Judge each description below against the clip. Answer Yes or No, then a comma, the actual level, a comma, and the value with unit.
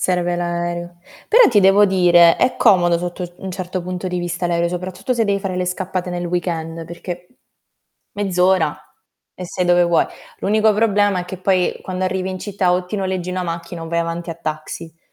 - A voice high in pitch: No, medium, 180 Hz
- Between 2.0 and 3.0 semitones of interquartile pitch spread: No, narrow, 1.6 semitones